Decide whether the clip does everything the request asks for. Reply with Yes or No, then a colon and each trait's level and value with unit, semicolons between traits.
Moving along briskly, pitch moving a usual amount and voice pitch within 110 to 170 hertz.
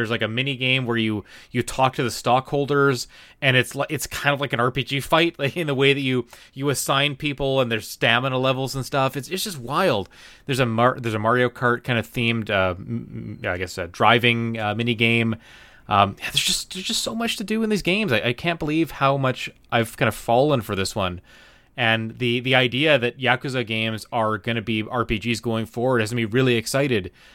Yes: fast, 225 wpm; average, 3.3 semitones; low, 125 Hz